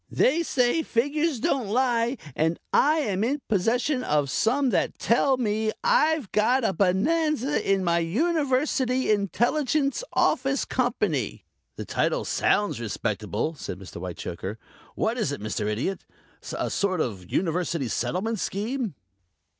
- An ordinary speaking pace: No, slow, 130 wpm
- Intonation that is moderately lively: No, wide, 8.0 semitones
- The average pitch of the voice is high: Yes, high, 225 Hz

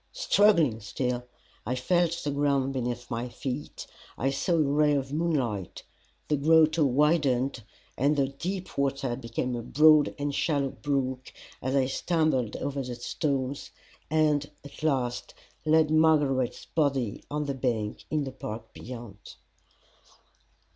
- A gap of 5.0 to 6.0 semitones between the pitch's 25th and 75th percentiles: No, average, 3.3 semitones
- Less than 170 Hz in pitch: Yes, medium, 140 Hz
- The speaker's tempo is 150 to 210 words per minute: No, slow, 135 wpm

